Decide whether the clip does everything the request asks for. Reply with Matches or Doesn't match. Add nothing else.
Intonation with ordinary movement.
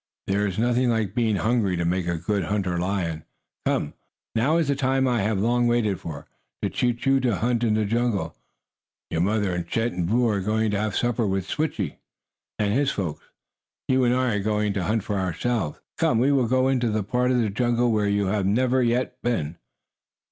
Matches